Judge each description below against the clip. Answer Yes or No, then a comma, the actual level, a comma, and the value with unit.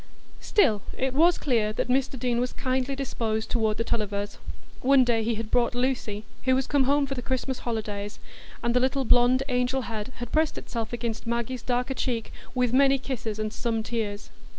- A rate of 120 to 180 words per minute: No, average, 190 wpm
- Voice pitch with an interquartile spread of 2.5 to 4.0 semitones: Yes, average, 2.8 semitones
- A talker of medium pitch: No, high, 245 Hz